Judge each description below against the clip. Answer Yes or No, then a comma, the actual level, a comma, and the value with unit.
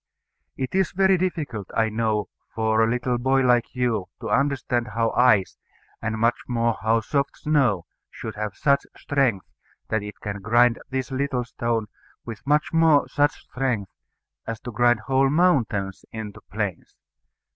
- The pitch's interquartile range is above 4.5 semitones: No, average, 3.7 semitones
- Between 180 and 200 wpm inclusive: No, average, 150 wpm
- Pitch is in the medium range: No, low, 120 Hz